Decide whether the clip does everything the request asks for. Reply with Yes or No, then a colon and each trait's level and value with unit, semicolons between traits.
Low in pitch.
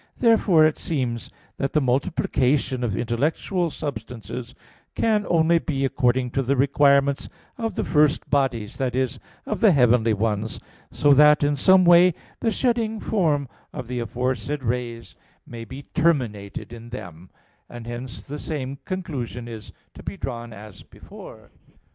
Yes: low, 130 Hz